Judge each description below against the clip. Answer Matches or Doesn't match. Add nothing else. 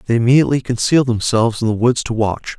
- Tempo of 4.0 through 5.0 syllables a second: Doesn't match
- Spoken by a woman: Doesn't match